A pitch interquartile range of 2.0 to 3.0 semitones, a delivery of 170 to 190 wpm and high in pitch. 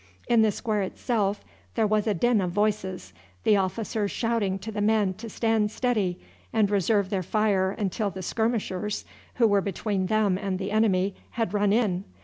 Yes: narrow, 2.4 semitones; average, 175 wpm; high, 205 Hz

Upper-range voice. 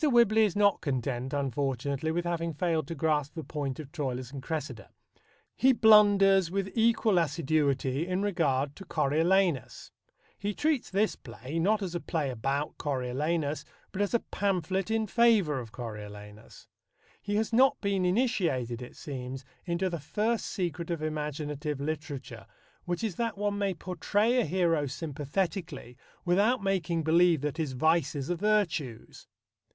No: medium, 165 Hz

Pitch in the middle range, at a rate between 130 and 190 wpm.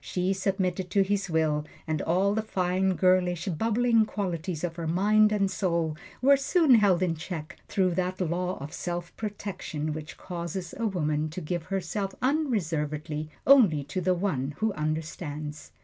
Yes: medium, 180 Hz; average, 160 wpm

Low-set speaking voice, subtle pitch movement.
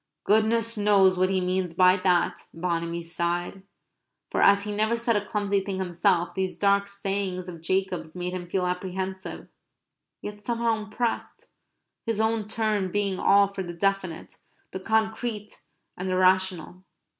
No: high, 190 Hz; narrow, 2.3 semitones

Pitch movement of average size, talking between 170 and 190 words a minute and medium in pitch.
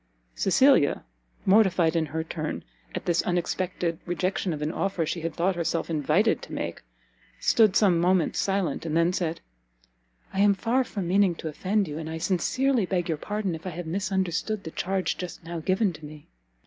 Yes: average, 3.0 semitones; average, 185 wpm; medium, 175 Hz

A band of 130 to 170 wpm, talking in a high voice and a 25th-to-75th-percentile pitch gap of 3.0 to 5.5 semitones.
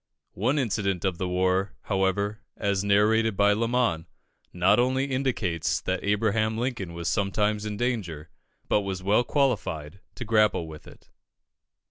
No: average, 140 wpm; low, 100 Hz; average, 3.3 semitones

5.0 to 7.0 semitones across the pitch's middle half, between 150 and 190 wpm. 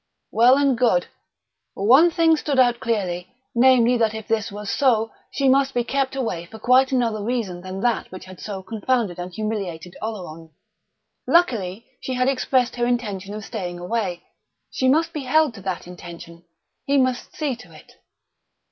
Yes: wide, 5.5 semitones; average, 170 wpm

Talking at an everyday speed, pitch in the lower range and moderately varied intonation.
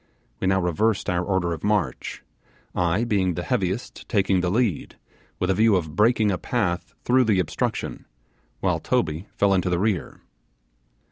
Yes: average, 160 wpm; very low, 95 Hz; average, 3.4 semitones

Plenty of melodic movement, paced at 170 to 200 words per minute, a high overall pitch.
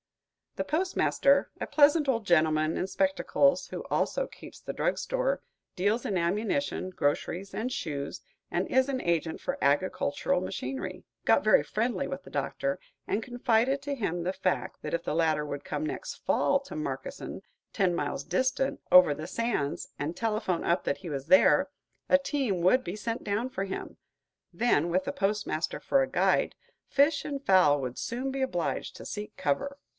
Yes: wide, 8.2 semitones; average, 175 wpm; high, 205 Hz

